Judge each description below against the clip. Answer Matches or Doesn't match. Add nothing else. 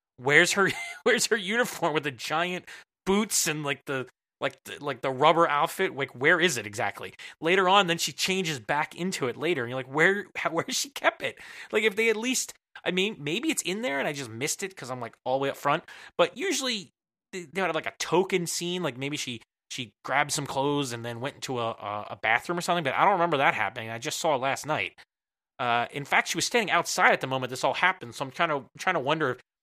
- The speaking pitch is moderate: Matches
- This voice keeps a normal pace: Doesn't match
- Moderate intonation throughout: Doesn't match